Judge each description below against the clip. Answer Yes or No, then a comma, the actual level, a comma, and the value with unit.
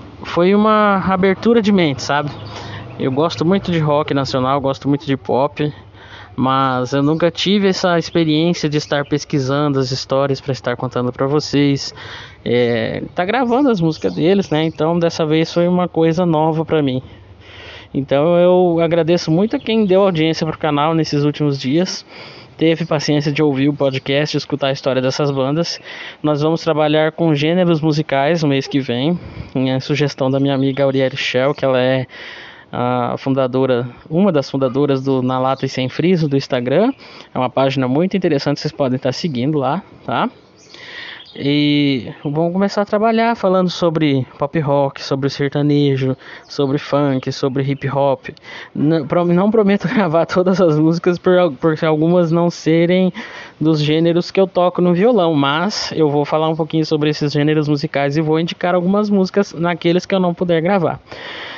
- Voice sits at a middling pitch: Yes, medium, 150 Hz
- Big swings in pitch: No, average, 4.0 semitones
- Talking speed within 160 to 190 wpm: Yes, average, 170 wpm